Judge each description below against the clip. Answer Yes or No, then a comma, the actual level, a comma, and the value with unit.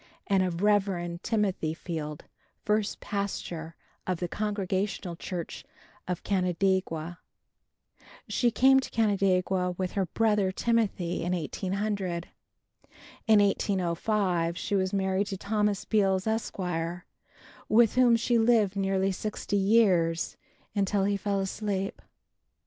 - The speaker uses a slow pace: Yes, slow, 115 wpm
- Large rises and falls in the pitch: No, narrow, 2.5 semitones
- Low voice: No, high, 195 Hz